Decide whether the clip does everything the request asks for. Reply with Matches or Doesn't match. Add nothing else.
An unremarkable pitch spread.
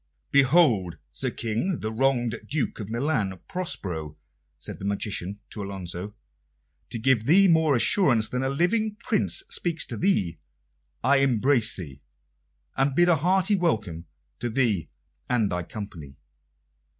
Doesn't match